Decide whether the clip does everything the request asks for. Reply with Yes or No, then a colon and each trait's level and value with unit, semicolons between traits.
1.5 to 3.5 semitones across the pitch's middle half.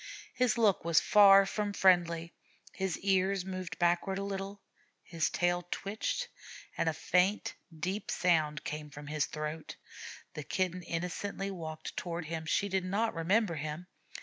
Yes: average, 3.2 semitones